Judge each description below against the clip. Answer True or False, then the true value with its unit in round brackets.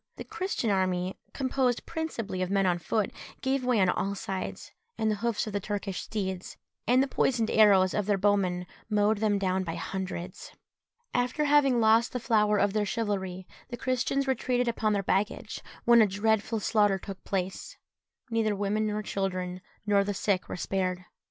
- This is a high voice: True (205 Hz)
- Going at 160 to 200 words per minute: True (175 wpm)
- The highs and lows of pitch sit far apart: False (3.3 semitones)